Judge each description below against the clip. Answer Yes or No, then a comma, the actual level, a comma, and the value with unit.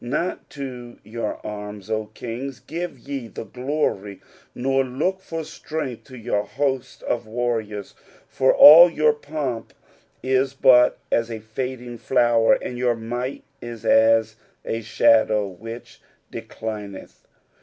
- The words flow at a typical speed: No, slow, 130 wpm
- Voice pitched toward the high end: No, low, 120 Hz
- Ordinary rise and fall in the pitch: Yes, average, 3.3 semitones